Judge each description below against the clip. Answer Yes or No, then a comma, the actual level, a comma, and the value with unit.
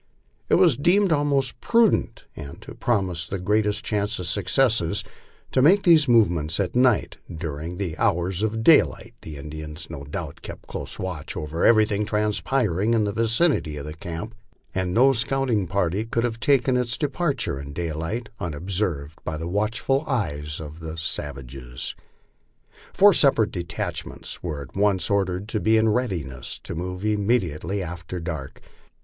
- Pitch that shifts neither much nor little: No, wide, 6.0 semitones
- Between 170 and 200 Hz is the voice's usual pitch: No, low, 100 Hz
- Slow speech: No, average, 155 wpm